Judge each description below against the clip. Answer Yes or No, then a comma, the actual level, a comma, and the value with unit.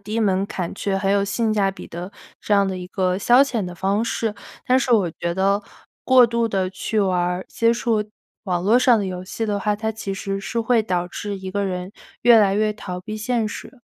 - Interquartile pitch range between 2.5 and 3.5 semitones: Yes, average, 2.9 semitones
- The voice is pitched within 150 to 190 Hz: No, high, 200 Hz